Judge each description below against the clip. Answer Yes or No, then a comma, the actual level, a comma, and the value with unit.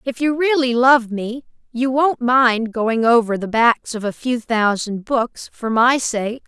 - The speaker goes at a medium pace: Yes, average, 185 wpm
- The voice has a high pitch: Yes, high, 240 Hz